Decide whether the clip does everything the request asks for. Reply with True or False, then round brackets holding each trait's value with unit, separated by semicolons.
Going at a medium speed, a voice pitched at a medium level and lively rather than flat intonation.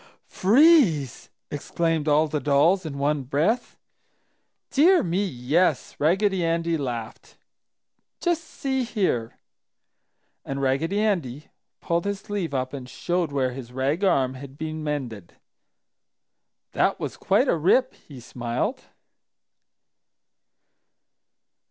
False (110 wpm; 155 Hz; 6.2 semitones)